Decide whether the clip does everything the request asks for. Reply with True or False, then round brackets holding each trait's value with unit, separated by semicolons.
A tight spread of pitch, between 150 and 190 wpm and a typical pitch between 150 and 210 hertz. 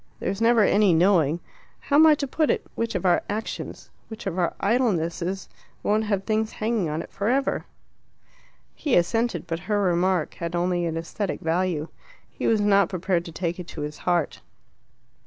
False (4.1 semitones; 180 wpm; 190 Hz)